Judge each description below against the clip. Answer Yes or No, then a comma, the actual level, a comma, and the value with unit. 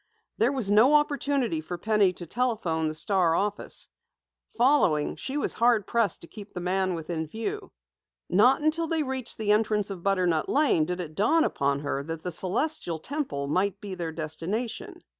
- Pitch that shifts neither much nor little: No, wide, 7.1 semitones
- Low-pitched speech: No, high, 200 Hz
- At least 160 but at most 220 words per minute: Yes, average, 175 wpm